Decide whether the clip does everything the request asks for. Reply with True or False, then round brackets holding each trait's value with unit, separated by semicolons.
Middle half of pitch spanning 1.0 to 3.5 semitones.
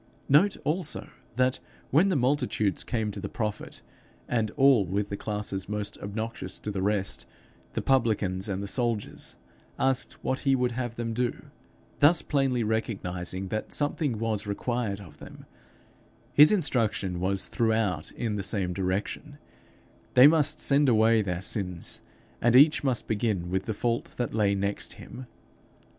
False (4.3 semitones)